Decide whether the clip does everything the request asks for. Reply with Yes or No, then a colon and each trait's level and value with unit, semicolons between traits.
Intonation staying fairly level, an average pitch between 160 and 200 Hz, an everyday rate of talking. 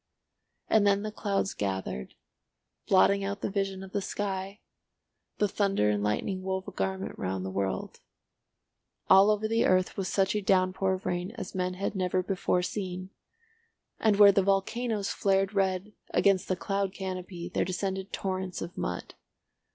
Yes: narrow, 1.5 semitones; high, 190 Hz; average, 160 wpm